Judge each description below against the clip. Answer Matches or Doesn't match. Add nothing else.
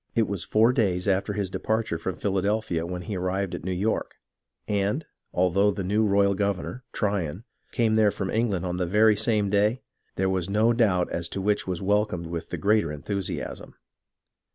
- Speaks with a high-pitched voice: Doesn't match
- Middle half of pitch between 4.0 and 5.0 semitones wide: Doesn't match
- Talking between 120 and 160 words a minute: Doesn't match